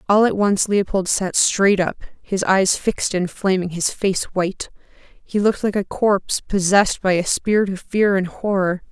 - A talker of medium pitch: No, high, 195 Hz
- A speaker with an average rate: Yes, average, 190 wpm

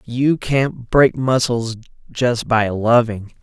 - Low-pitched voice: Yes, low, 120 Hz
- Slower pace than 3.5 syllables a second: Yes, 3.0 syllables/s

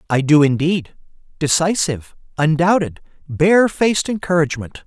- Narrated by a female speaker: No, male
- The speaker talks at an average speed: No, slow, 85 wpm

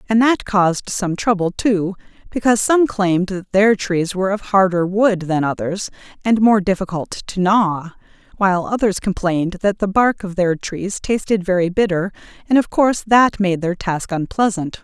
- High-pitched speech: Yes, high, 195 Hz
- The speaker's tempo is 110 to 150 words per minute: No, average, 165 wpm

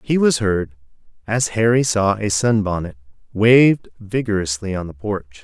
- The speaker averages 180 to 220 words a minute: No, average, 145 wpm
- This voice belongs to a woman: No, male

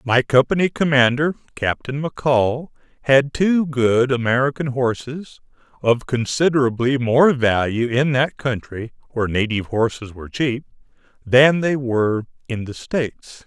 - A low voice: Yes, low, 130 Hz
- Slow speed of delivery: Yes, slow, 125 wpm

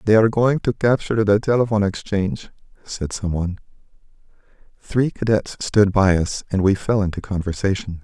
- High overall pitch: No, low, 100 Hz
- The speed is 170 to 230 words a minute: No, average, 155 wpm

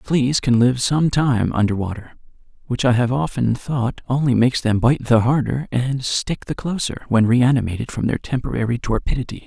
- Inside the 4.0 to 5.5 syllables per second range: Yes, 5.0 syllables/s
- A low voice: Yes, low, 125 Hz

